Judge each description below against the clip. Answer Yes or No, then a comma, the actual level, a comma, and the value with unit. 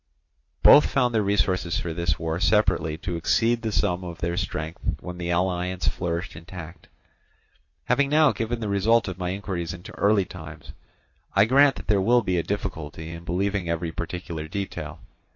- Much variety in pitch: No, average, 3.3 semitones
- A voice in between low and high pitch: No, very low, 90 Hz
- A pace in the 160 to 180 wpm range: Yes, average, 170 wpm